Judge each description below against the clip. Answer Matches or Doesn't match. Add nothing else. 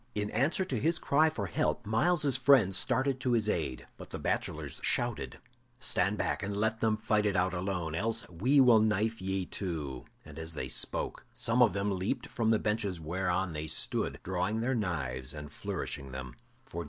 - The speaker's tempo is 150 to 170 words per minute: Doesn't match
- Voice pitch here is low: Matches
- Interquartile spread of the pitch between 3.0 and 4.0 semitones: Doesn't match